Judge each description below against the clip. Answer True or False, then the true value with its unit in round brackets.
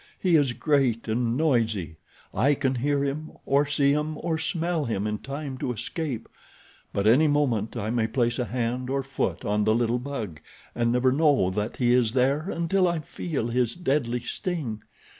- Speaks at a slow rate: False (180 wpm)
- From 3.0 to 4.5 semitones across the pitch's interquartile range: True (4.1 semitones)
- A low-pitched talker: True (130 Hz)